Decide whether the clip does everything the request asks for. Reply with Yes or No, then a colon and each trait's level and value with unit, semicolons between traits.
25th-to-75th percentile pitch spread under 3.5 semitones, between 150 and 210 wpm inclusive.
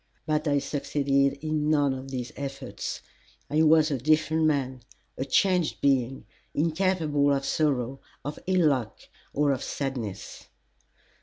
No: narrow, 2.5 semitones; slow, 135 wpm